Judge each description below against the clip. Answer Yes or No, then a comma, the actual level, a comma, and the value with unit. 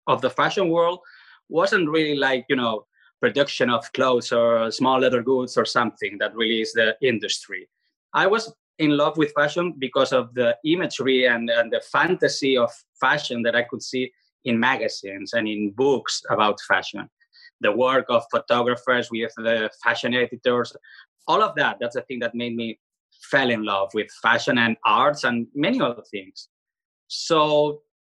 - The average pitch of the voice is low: Yes, low, 125 Hz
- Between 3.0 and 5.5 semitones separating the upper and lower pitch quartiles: Yes, average, 4.0 semitones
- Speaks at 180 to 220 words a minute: No, average, 170 wpm